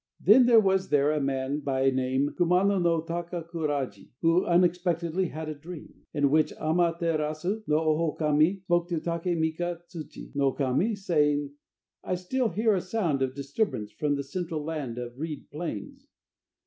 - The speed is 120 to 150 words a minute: No, average, 160 wpm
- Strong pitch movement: No, average, 3.5 semitones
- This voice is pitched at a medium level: Yes, medium, 160 Hz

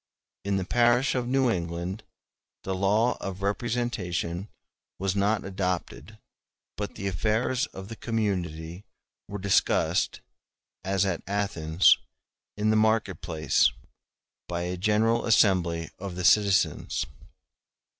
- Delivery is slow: Yes, slow, 120 wpm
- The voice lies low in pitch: Yes, low, 100 Hz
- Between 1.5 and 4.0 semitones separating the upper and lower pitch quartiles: Yes, average, 3.5 semitones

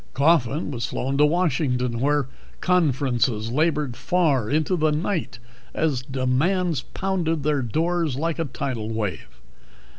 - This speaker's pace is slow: Yes, slow, 125 wpm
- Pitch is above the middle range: No, medium, 145 Hz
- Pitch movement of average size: Yes, average, 4.7 semitones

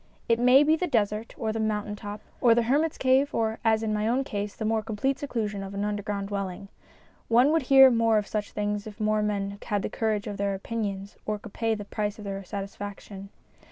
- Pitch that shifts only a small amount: Yes, narrow, 2.2 semitones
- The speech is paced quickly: Yes, fast, 225 wpm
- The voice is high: Yes, high, 215 Hz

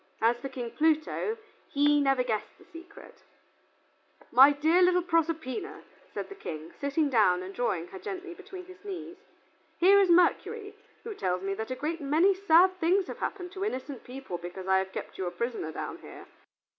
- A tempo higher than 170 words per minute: Yes, average, 180 wpm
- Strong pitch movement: Yes, wide, 7.7 semitones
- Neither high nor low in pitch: No, very high, 300 Hz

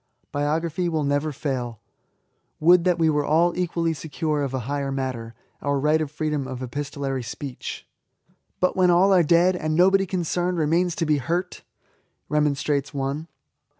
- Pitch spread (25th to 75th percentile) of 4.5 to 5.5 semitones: No, average, 3.5 semitones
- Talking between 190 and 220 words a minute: No, average, 170 wpm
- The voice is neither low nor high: Yes, medium, 150 Hz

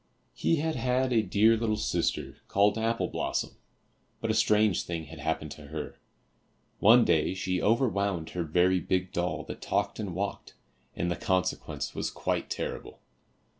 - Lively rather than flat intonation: No, average, 4.4 semitones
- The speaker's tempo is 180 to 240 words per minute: No, average, 165 wpm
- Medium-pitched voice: No, very low, 95 Hz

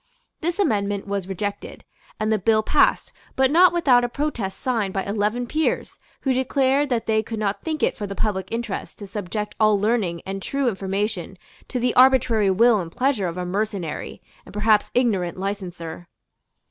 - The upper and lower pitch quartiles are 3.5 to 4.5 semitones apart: Yes, average, 4.0 semitones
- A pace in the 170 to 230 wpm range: Yes, average, 175 wpm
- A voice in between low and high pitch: No, high, 215 Hz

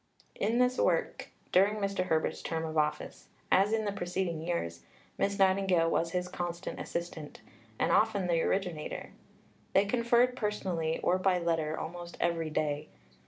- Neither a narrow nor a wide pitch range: Yes, average, 3.3 semitones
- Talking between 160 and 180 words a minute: No, average, 150 wpm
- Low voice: No, medium, 180 Hz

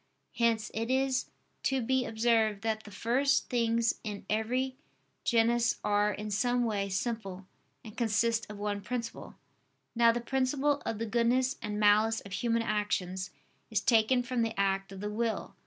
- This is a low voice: No, high, 225 Hz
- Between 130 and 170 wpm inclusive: Yes, average, 160 wpm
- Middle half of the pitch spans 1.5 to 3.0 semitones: Yes, narrow, 2.5 semitones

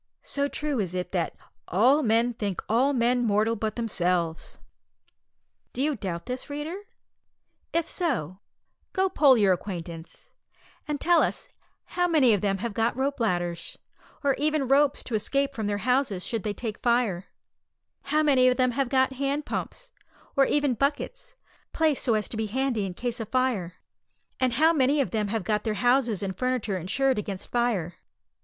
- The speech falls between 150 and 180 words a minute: Yes, average, 175 wpm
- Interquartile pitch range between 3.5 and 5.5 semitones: Yes, average, 5.2 semitones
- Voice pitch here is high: Yes, high, 245 Hz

